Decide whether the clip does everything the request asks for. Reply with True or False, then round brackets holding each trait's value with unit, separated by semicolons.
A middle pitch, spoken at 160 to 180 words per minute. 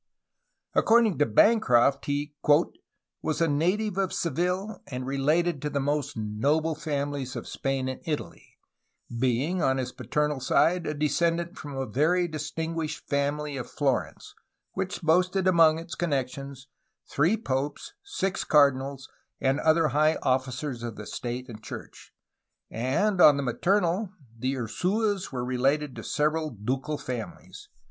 False (150 Hz; 140 wpm)